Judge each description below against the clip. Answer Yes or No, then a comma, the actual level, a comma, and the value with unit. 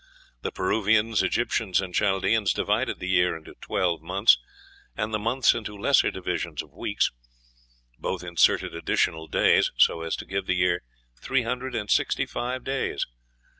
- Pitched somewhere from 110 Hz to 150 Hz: No, low, 100 Hz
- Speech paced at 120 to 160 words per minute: Yes, average, 155 wpm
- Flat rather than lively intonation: No, average, 4.2 semitones